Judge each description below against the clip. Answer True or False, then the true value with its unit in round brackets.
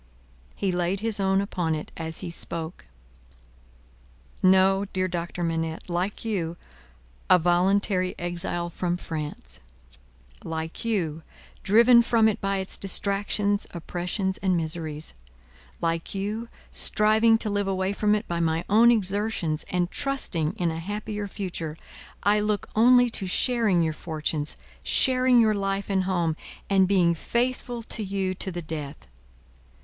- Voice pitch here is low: False (190 Hz)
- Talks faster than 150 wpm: False (140 wpm)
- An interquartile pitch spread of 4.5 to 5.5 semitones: False (3.6 semitones)